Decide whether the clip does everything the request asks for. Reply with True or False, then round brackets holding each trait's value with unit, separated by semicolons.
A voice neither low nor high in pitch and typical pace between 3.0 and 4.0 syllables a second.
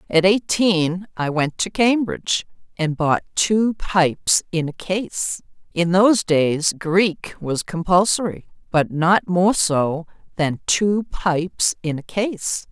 True (180 Hz; 3.5 syllables/s)